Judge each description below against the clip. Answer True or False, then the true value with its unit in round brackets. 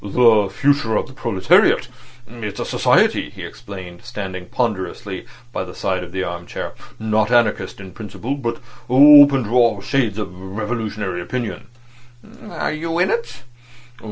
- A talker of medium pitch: False (110 Hz)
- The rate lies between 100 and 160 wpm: True (150 wpm)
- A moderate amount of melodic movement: True (4.7 semitones)